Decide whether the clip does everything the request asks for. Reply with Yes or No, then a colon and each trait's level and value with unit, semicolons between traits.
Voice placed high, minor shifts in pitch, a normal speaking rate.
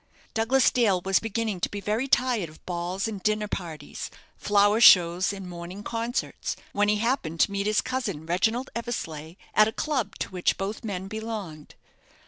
No: high, 205 Hz; average, 3.9 semitones; average, 170 wpm